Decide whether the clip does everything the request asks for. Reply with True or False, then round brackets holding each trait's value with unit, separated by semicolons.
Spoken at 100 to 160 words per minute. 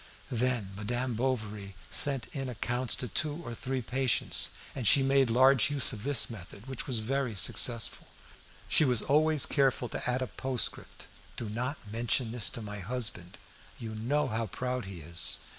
False (170 wpm)